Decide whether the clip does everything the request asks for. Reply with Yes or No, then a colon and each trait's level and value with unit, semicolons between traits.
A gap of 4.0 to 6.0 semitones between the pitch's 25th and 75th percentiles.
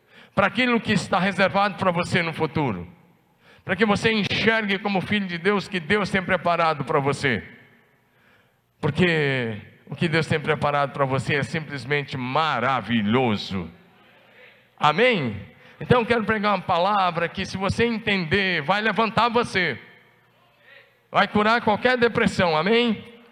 Yes: wide, 5.5 semitones